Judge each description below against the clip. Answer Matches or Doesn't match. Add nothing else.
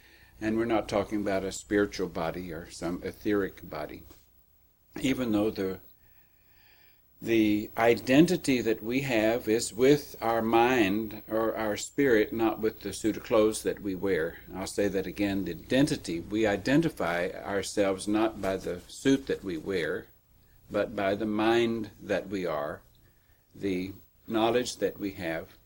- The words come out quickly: Doesn't match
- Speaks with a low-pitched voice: Matches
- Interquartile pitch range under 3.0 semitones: Matches